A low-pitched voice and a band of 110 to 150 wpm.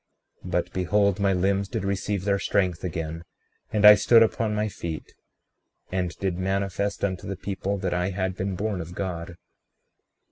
No: very low, 95 Hz; average, 170 wpm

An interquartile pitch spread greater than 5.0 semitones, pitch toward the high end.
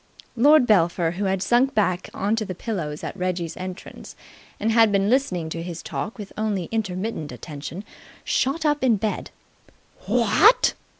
No: average, 4.1 semitones; high, 200 Hz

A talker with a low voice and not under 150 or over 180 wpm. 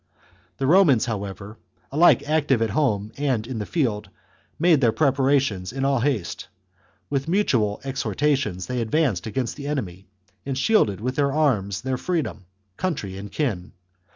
Yes: low, 130 Hz; average, 155 wpm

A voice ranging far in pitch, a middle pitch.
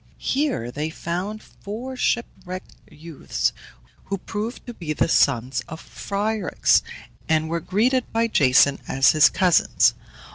Yes: wide, 6.2 semitones; medium, 180 Hz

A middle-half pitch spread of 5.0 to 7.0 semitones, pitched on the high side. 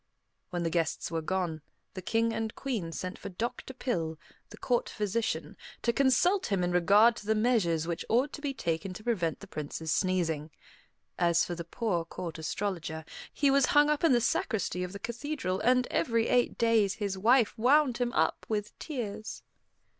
Yes: wide, 5.6 semitones; high, 210 Hz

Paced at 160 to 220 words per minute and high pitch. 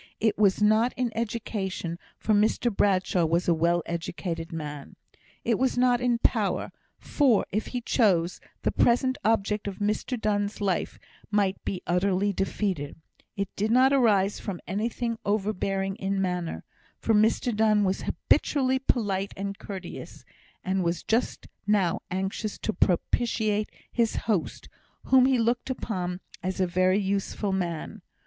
No: average, 145 wpm; high, 205 Hz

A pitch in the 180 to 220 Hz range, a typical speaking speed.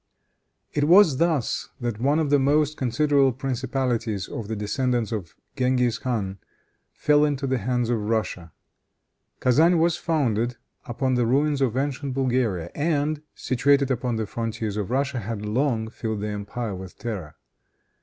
No: low, 125 Hz; average, 150 wpm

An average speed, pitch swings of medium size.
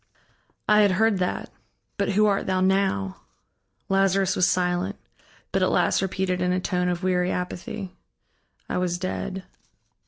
No: average, 150 wpm; narrow, 1.4 semitones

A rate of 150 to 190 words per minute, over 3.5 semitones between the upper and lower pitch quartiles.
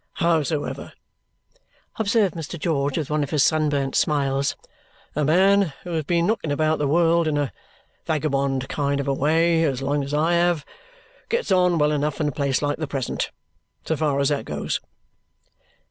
No: average, 175 wpm; average, 2.9 semitones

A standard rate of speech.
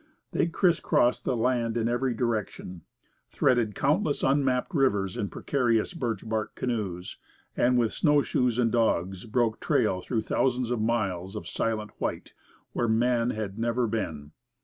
Yes: average, 145 wpm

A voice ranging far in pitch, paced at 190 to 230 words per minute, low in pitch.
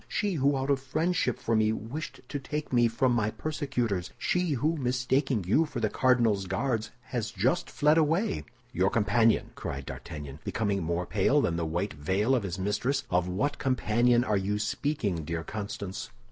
No: wide, 5.9 semitones; average, 175 wpm; low, 115 Hz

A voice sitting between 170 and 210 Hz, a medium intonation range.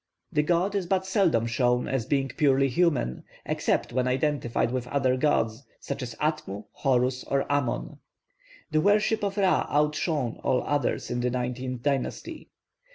No: low, 135 Hz; average, 3.8 semitones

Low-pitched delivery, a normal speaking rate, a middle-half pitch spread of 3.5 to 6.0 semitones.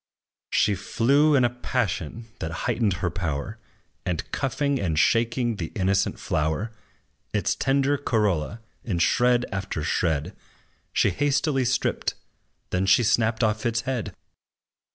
No: low, 110 Hz; slow, 130 wpm; average, 5.2 semitones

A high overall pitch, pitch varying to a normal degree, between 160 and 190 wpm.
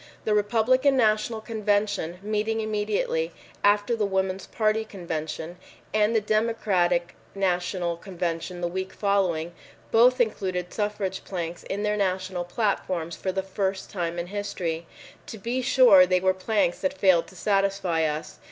No: high, 195 Hz; average, 3.3 semitones; average, 145 wpm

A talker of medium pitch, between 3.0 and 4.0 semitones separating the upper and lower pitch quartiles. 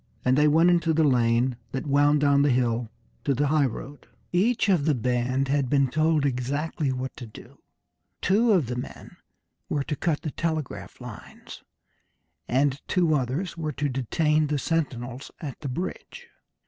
Yes: medium, 145 Hz; average, 3.6 semitones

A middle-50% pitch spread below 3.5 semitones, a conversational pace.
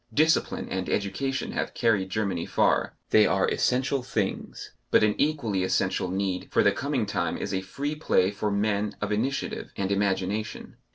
No: average, 4.6 semitones; average, 165 wpm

